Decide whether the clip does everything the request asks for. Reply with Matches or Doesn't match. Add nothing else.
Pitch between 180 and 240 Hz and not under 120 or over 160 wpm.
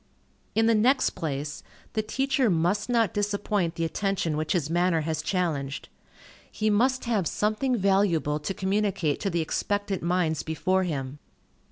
Matches